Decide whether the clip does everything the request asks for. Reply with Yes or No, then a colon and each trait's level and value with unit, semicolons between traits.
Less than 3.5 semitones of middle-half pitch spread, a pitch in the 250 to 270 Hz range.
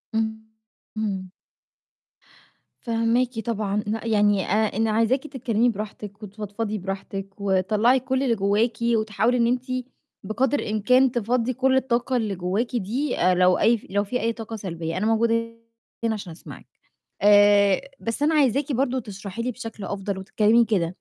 No: average, 2.9 semitones; high, 220 Hz